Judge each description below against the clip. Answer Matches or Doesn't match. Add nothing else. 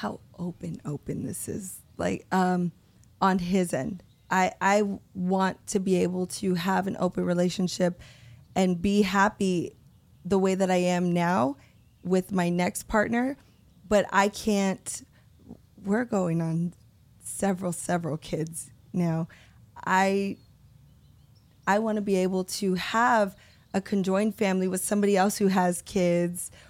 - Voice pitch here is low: Doesn't match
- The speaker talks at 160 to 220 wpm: Doesn't match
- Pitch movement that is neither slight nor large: Doesn't match